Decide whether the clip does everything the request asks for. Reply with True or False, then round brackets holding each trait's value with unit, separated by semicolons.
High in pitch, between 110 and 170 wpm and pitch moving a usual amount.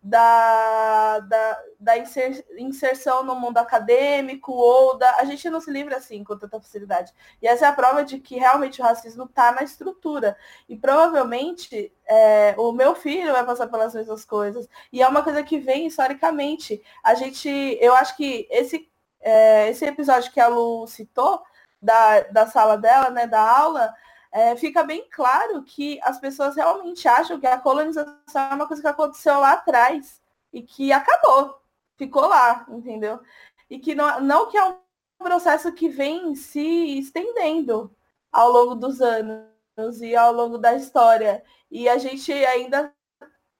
True (260 Hz; 165 wpm; 4.3 semitones)